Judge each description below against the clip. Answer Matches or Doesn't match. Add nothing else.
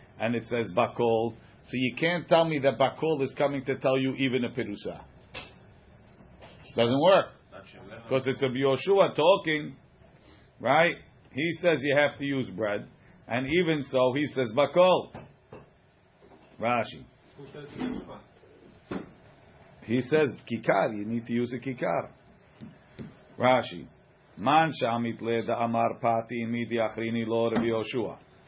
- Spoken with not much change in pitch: Doesn't match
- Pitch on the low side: Matches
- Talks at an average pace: Doesn't match